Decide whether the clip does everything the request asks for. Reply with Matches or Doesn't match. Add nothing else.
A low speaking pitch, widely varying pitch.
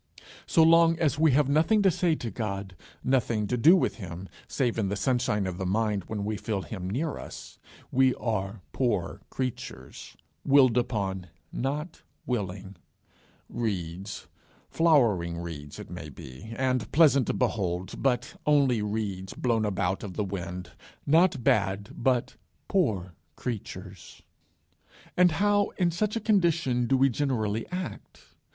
Matches